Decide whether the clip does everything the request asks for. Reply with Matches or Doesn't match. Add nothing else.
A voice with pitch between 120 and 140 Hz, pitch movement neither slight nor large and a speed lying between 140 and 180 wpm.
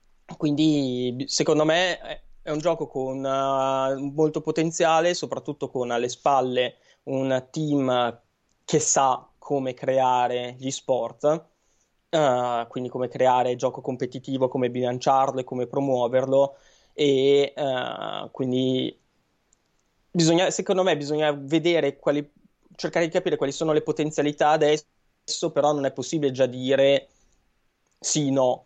Doesn't match